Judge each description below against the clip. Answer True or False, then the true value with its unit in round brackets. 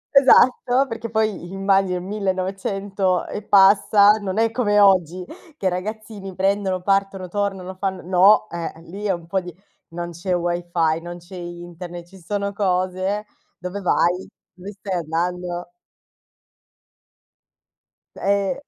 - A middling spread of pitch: False (2.3 semitones)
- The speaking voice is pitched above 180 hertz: True (190 Hz)